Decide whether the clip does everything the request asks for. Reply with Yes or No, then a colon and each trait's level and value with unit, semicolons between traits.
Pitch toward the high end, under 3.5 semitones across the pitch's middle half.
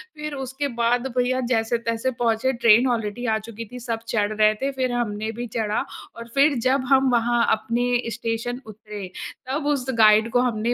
Yes: high, 235 Hz; narrow, 2.4 semitones